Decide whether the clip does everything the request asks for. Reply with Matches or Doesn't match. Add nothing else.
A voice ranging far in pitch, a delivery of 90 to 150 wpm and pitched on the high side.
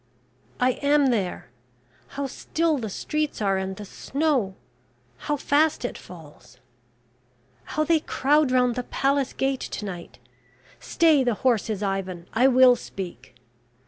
Matches